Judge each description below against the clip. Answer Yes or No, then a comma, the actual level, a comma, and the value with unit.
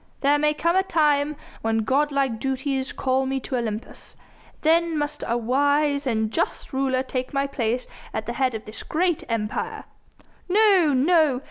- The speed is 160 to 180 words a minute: Yes, average, 165 wpm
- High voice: Yes, very high, 275 Hz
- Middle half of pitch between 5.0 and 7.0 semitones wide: No, average, 3.3 semitones